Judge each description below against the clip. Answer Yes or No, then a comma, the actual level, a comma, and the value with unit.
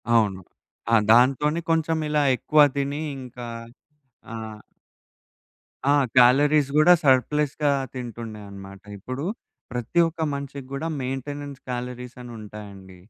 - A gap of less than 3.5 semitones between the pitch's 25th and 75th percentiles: No, average, 4.1 semitones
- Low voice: Yes, low, 130 Hz